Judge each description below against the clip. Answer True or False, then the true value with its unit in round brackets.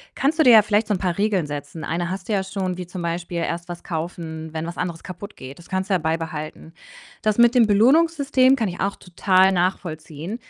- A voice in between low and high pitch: True (180 Hz)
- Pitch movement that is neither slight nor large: True (4.0 semitones)